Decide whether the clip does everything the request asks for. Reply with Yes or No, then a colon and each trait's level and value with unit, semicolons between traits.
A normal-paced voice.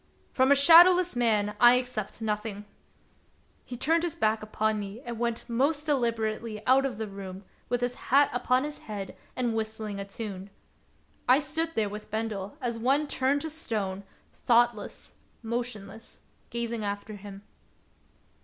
Yes: average, 155 wpm